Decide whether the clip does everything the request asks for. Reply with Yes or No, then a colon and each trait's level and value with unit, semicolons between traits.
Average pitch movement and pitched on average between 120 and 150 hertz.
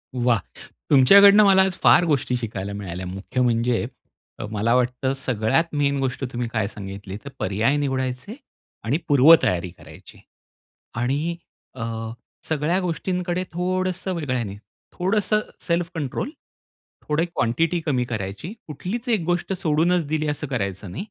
No: wide, 7.0 semitones; medium, 140 Hz